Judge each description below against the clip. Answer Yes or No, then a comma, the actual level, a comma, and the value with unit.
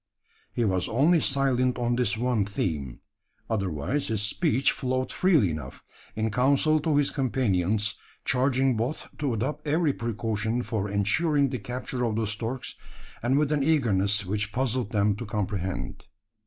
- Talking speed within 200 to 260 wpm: No, average, 150 wpm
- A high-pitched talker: No, low, 120 Hz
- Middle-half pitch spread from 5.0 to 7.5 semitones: No, average, 4.5 semitones